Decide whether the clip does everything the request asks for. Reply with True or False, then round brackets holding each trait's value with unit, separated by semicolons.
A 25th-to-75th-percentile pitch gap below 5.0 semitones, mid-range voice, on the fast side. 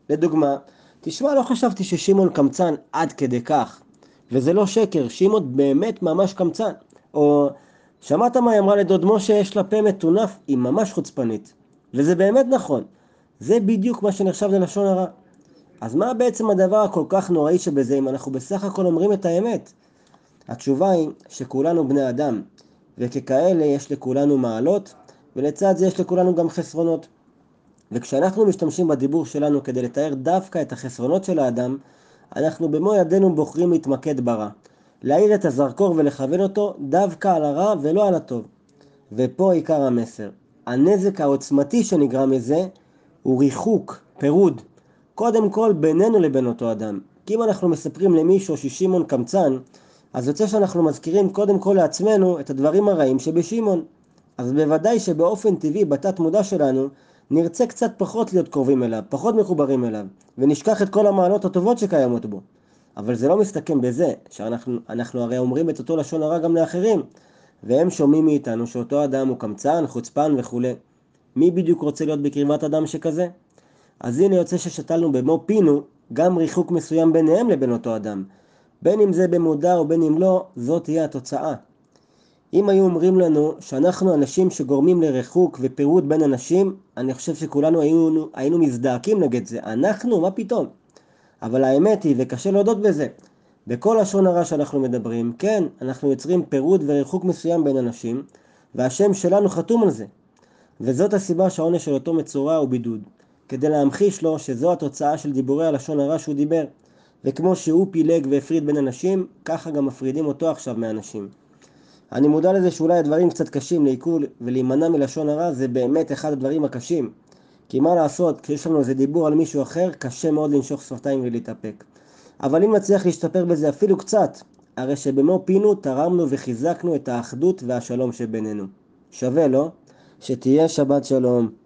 False (5.3 semitones; 160 Hz; 155 wpm)